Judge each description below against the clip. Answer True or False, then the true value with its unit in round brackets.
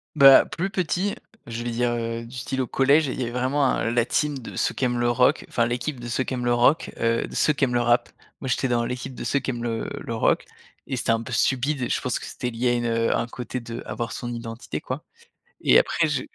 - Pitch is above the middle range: False (120 Hz)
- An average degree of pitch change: False (2.1 semitones)